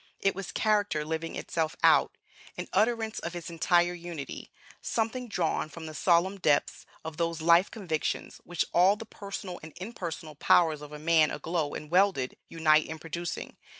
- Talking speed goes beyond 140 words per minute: Yes, average, 165 wpm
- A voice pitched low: No, medium, 170 Hz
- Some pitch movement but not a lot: Yes, average, 3.5 semitones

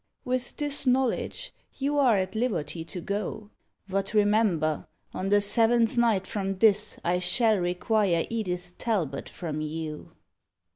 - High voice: Yes, high, 205 Hz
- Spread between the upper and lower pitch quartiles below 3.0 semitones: No, average, 4.5 semitones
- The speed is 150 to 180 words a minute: No, slow, 135 wpm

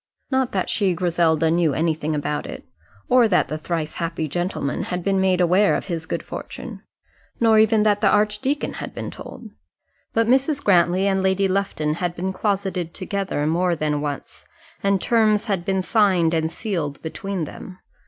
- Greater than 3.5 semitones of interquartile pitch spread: Yes, average, 3.9 semitones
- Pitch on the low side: No, medium, 185 Hz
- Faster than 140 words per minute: Yes, average, 170 wpm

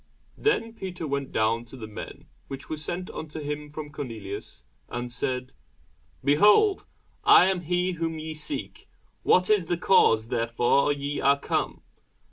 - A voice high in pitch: No, medium, 150 Hz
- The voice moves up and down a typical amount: No, wide, 5.8 semitones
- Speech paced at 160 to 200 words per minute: No, average, 150 wpm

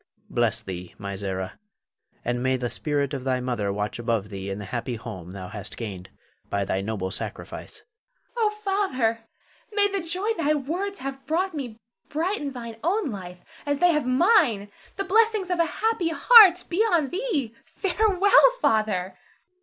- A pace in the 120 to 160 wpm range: No, average, 170 wpm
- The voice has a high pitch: Yes, very high, 255 Hz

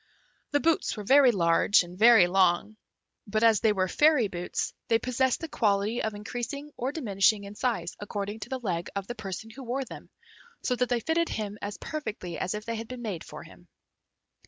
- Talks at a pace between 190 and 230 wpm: Yes, fast, 205 wpm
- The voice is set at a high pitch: Yes, high, 220 Hz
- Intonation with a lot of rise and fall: No, average, 4.0 semitones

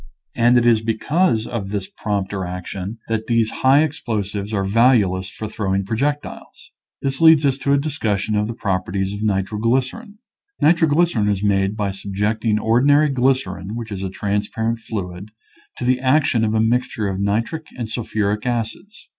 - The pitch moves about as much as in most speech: Yes, average, 4.2 semitones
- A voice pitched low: Yes, low, 110 Hz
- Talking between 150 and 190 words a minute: Yes, average, 165 wpm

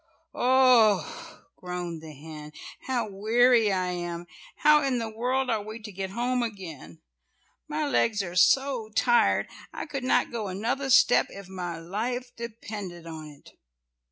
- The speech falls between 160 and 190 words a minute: No, average, 150 wpm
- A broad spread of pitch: Yes, wide, 5.8 semitones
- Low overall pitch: No, high, 215 Hz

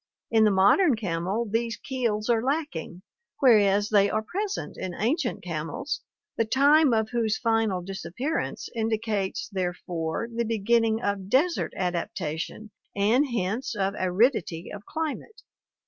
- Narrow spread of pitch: No, average, 4.2 semitones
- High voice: Yes, high, 220 Hz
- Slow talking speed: Yes, slow, 130 wpm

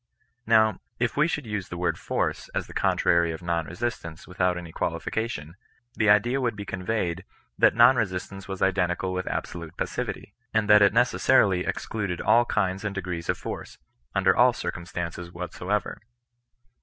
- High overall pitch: No, very low, 95 Hz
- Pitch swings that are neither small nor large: Yes, average, 3.8 semitones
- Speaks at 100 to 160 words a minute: Yes, average, 155 wpm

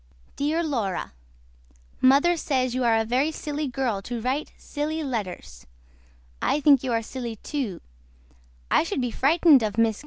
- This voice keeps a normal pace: Yes, average, 160 wpm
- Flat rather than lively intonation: No, average, 4.5 semitones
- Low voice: No, very high, 260 Hz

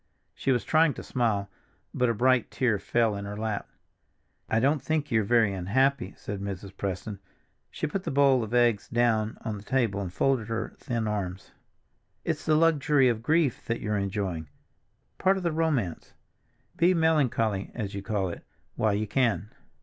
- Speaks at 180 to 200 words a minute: No, average, 165 wpm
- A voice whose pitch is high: No, low, 115 Hz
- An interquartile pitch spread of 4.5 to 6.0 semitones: Yes, average, 5.1 semitones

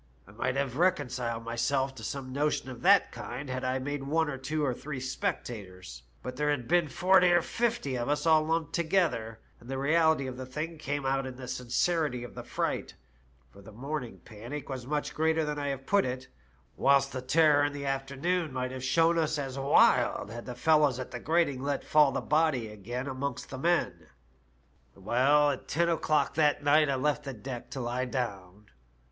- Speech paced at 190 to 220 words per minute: Yes, average, 200 wpm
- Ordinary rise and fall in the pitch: Yes, average, 3.4 semitones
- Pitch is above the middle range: No, low, 135 Hz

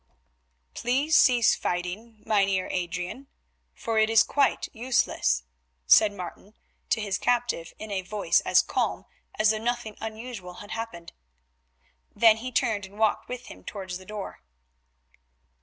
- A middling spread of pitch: Yes, average, 3.7 semitones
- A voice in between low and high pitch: No, high, 215 Hz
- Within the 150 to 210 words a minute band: No, average, 140 wpm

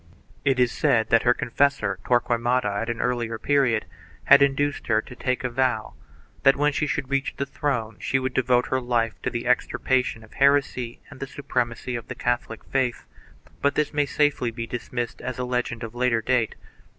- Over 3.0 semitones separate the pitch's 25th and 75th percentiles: No, narrow, 2.6 semitones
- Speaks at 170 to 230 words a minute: Yes, average, 195 wpm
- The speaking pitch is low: Yes, low, 125 Hz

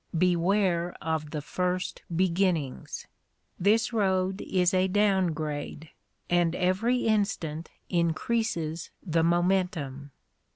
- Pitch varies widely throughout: No, average, 2.8 semitones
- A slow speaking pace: Yes, slow, 95 wpm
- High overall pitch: No, medium, 180 Hz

